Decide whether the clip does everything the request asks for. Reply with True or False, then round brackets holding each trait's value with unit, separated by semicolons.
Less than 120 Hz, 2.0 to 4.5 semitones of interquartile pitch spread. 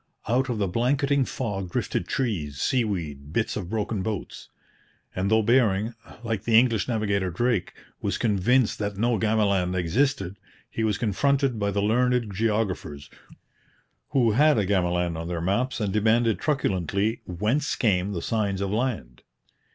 True (105 Hz; 4.0 semitones)